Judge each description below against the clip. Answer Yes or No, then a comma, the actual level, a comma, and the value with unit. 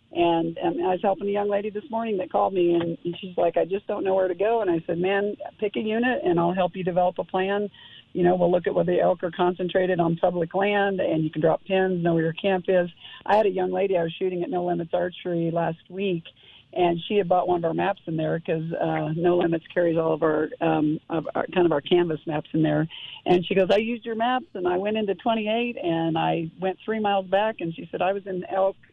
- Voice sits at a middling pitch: Yes, medium, 180 Hz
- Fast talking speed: Yes, fast, 265 wpm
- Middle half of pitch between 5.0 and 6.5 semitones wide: No, average, 2.7 semitones